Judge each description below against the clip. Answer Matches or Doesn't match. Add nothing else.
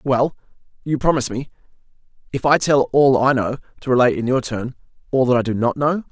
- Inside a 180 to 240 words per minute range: Matches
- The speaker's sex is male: Matches